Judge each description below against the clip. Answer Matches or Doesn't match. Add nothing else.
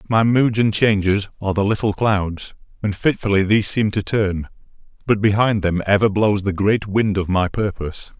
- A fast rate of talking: Doesn't match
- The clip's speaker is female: Doesn't match